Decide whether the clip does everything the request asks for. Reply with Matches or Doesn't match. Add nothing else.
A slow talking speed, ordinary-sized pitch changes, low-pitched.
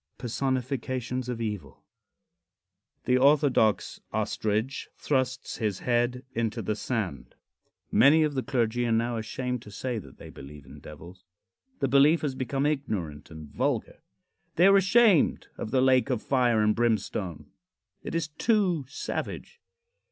Doesn't match